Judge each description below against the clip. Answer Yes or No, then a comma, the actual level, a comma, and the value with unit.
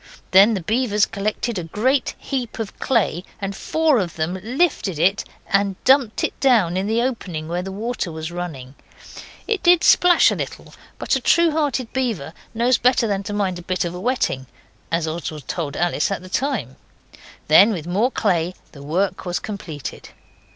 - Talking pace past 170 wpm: Yes, average, 180 wpm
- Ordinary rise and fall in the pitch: No, wide, 6.0 semitones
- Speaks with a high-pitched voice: Yes, high, 200 Hz